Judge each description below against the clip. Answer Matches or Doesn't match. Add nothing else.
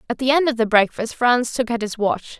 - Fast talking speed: Matches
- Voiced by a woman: Matches